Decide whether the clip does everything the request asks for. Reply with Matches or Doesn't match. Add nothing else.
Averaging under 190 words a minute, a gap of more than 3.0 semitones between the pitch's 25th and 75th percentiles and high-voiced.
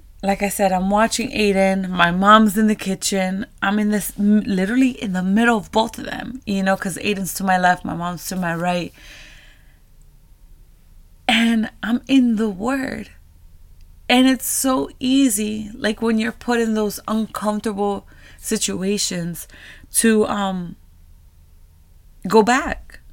Matches